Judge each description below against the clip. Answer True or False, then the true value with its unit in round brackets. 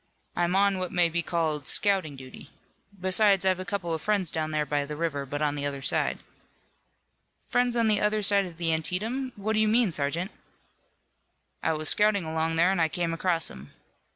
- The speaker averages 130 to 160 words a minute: False (200 wpm)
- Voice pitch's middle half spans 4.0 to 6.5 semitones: True (4.4 semitones)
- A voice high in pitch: False (175 Hz)